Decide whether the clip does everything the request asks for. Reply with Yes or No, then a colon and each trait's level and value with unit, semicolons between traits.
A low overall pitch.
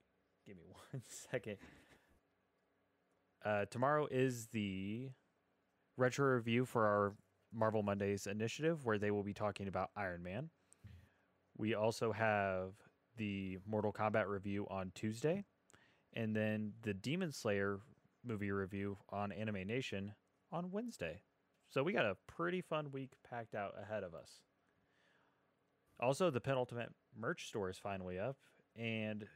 Yes: low, 105 Hz